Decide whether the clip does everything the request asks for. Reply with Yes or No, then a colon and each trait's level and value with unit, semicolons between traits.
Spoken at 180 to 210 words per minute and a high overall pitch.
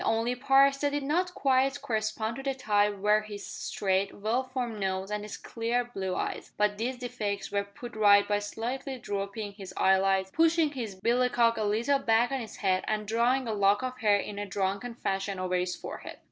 Yes: average, 200 wpm; high, 220 Hz